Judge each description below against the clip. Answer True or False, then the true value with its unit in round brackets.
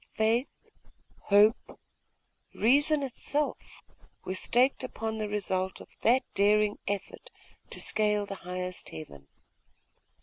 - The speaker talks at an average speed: False (105 wpm)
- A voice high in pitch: True (210 Hz)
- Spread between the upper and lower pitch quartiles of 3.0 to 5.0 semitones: True (4.1 semitones)